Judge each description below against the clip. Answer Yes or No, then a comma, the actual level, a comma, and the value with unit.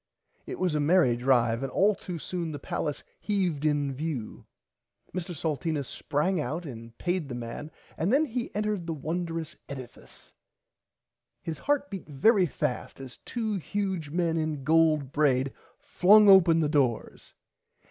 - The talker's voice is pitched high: No, medium, 160 Hz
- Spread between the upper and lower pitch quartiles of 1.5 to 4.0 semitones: No, average, 4.7 semitones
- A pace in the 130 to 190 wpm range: Yes, average, 150 wpm